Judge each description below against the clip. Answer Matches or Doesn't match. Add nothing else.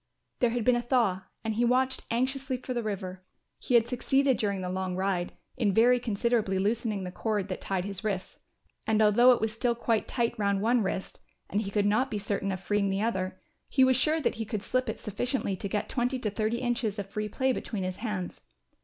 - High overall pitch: Matches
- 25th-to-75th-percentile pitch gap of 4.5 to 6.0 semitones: Doesn't match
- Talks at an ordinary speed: Doesn't match